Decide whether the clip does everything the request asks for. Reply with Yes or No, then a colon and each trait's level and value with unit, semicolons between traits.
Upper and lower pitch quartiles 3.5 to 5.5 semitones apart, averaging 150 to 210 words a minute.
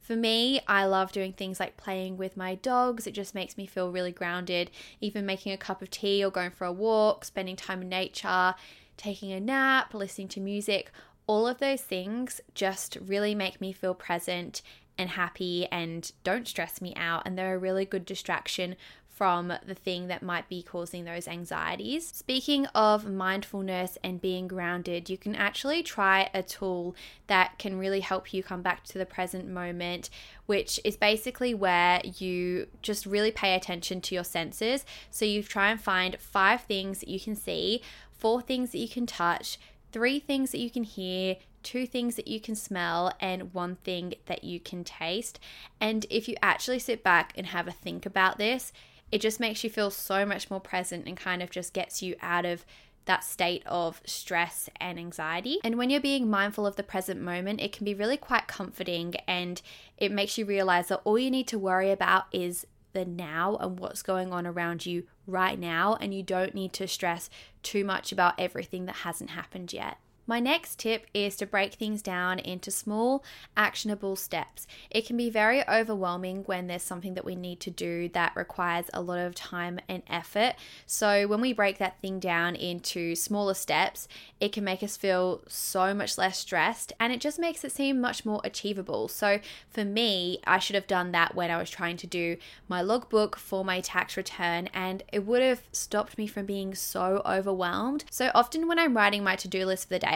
No: average, 2.9 semitones; average, 200 wpm